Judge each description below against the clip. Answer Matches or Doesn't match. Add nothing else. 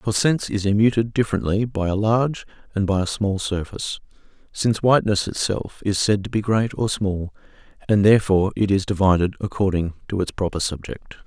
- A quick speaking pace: Doesn't match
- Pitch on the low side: Matches